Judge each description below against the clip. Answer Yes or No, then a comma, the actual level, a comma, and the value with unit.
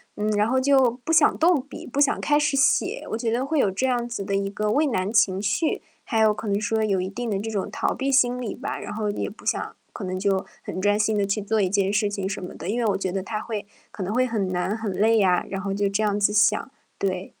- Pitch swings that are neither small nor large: Yes, average, 3.3 semitones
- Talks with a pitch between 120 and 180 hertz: No, high, 210 Hz